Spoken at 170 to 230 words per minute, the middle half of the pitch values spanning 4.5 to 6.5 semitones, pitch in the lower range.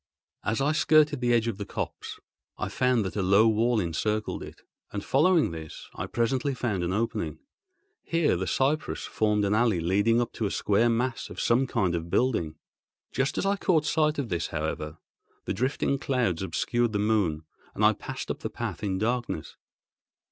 Yes: average, 185 wpm; average, 5.2 semitones; low, 115 Hz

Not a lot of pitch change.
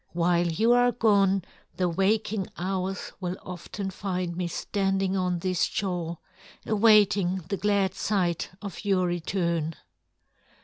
Yes: narrow, 2.3 semitones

